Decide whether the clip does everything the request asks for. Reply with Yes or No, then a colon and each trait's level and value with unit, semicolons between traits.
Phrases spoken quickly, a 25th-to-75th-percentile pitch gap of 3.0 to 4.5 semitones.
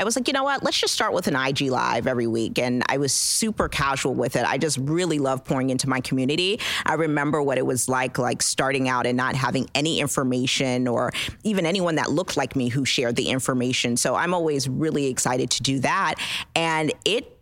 Yes: fast, 225 wpm; average, 3.7 semitones